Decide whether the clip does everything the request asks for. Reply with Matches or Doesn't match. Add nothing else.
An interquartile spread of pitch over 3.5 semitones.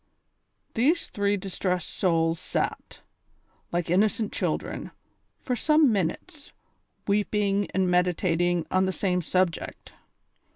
Doesn't match